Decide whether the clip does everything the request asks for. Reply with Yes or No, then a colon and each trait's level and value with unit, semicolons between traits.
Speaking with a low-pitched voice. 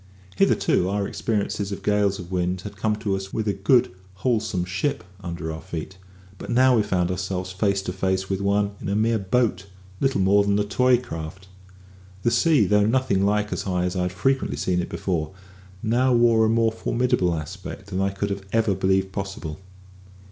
Yes: low, 100 Hz